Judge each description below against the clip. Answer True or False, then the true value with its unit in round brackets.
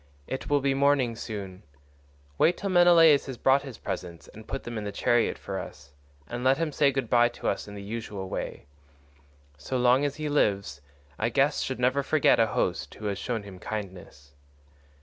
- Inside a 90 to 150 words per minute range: False (195 wpm)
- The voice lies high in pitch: False (120 Hz)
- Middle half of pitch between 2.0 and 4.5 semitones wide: False (5.4 semitones)